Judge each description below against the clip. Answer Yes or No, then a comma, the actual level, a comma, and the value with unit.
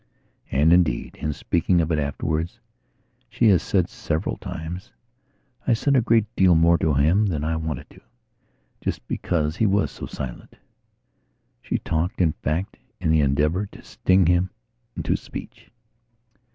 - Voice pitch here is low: Yes, very low, 85 Hz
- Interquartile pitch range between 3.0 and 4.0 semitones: Yes, average, 3.3 semitones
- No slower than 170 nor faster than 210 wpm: No, average, 150 wpm